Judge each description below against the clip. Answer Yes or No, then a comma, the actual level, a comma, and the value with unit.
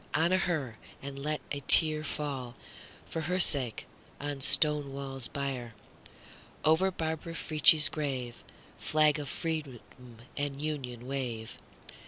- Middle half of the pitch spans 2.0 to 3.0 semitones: Yes, average, 2.7 semitones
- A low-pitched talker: No, medium, 145 Hz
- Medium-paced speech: No, slow, 105 wpm